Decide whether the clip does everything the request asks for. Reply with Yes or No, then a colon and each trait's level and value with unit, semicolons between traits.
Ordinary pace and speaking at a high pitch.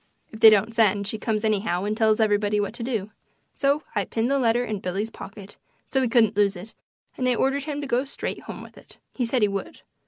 No: fast, 240 wpm; high, 220 Hz